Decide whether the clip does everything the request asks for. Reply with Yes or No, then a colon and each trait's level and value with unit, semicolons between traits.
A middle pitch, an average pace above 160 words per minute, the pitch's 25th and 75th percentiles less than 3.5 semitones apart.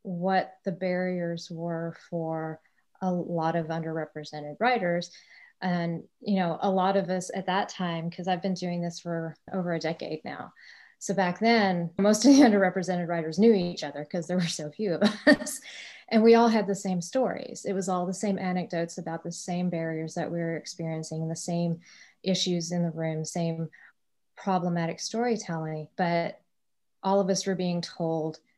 Yes: medium, 180 Hz; average, 180 wpm; average, 2.7 semitones